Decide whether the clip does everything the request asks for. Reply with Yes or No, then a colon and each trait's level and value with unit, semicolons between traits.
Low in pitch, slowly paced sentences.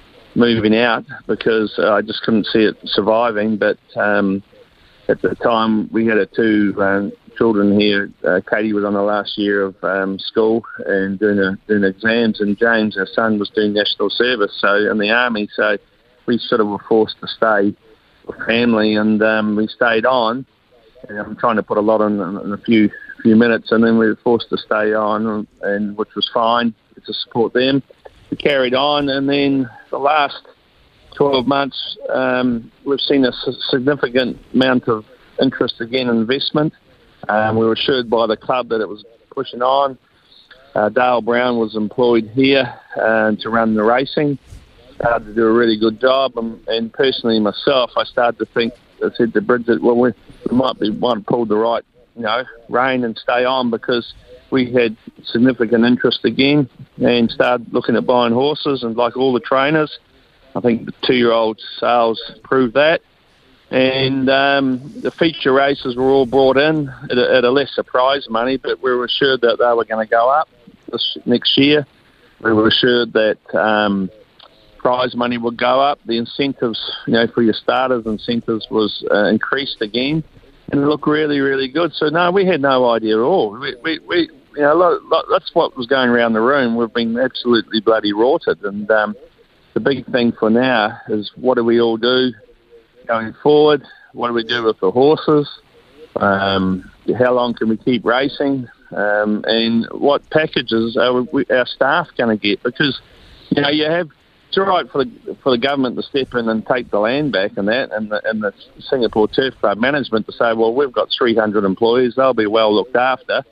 No: low, 115 Hz; average, 190 wpm